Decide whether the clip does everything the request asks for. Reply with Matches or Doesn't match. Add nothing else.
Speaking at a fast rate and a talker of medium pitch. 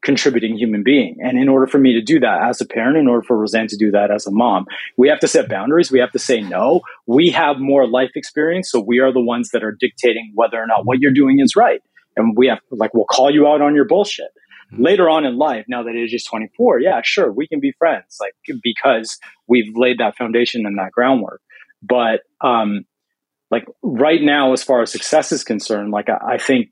Doesn't match